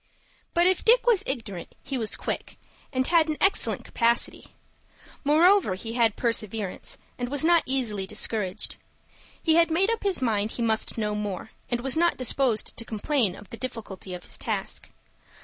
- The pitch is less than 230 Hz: No, high, 240 Hz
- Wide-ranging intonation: Yes, wide, 7.0 semitones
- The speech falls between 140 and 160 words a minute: No, average, 170 wpm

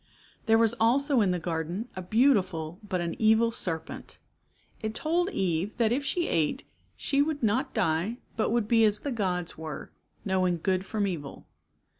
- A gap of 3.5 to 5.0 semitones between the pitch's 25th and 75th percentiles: Yes, average, 4.7 semitones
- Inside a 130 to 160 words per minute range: No, average, 170 wpm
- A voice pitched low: No, high, 210 Hz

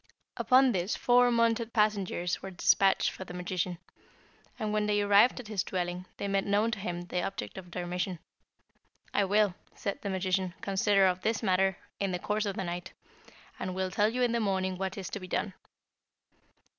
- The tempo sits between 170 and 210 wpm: Yes, average, 195 wpm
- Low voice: No, high, 195 Hz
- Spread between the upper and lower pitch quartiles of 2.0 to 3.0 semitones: Yes, narrow, 2.5 semitones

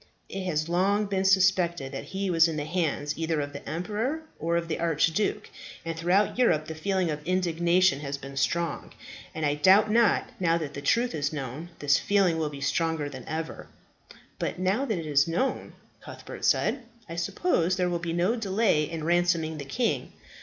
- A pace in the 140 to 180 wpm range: No, average, 190 wpm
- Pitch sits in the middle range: Yes, medium, 170 Hz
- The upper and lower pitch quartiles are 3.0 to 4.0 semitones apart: Yes, average, 3.7 semitones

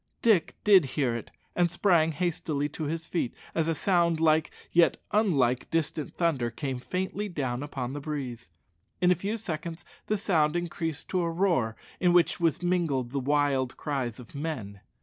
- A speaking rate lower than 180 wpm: Yes, average, 170 wpm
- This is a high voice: No, medium, 160 Hz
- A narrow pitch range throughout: No, average, 4.3 semitones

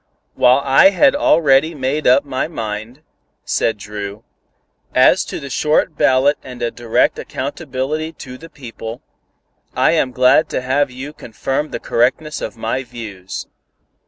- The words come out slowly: No, average, 145 wpm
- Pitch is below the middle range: Yes, low, 130 Hz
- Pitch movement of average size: Yes, average, 4.0 semitones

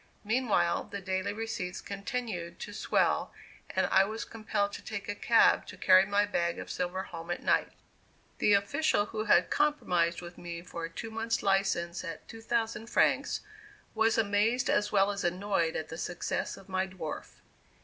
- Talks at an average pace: Yes, average, 170 wpm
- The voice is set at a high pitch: Yes, high, 200 Hz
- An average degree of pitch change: Yes, average, 3.9 semitones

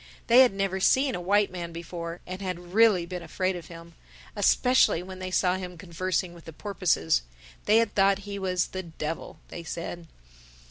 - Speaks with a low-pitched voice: No, medium, 185 Hz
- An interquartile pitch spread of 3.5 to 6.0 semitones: No, narrow, 2.6 semitones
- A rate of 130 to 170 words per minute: No, average, 180 wpm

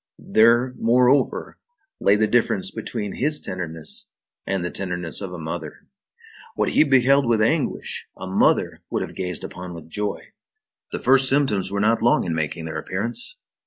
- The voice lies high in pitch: No, low, 105 Hz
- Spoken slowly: No, average, 160 wpm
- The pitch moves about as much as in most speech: No, wide, 6.1 semitones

